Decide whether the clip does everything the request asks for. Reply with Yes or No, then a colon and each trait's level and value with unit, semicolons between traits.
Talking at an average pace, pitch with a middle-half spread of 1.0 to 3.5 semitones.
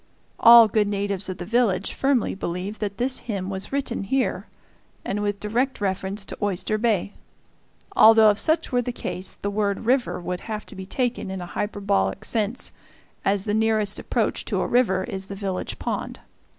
Yes: average, 180 wpm; average, 3.1 semitones